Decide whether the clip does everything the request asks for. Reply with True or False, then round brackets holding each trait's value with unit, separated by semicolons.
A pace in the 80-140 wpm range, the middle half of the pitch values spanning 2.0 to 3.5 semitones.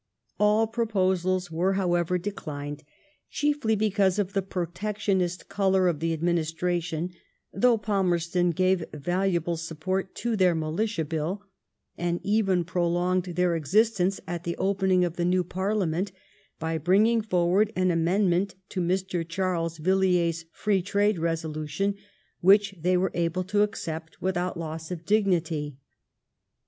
True (135 wpm; 2.7 semitones)